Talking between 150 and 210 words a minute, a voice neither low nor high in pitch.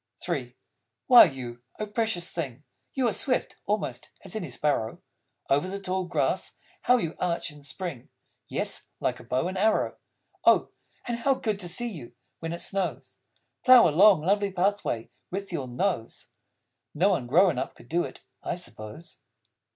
Yes: average, 165 wpm; medium, 175 Hz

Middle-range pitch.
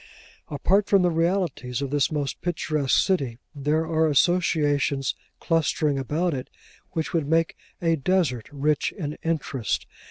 Yes: medium, 155 Hz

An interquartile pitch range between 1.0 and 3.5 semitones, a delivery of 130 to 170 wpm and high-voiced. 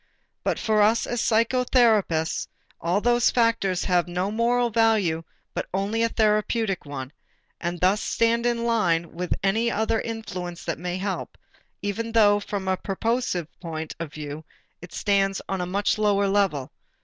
No: average, 4.2 semitones; average, 155 wpm; high, 200 Hz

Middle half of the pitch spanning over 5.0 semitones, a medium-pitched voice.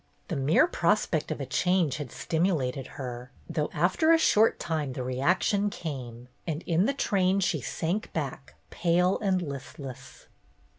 Yes: wide, 5.6 semitones; medium, 160 Hz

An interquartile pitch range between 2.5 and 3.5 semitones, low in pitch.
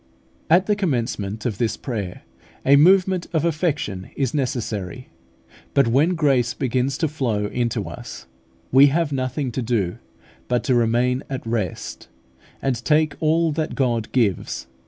No: average, 4.7 semitones; low, 130 Hz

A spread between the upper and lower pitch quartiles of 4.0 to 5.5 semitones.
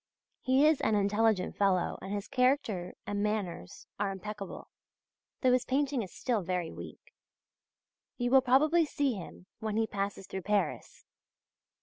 Yes: average, 4.7 semitones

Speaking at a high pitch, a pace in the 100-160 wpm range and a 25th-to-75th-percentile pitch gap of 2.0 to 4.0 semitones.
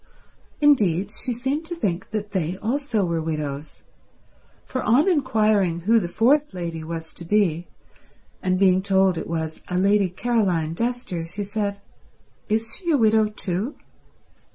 No: high, 200 Hz; average, 150 wpm; average, 5.0 semitones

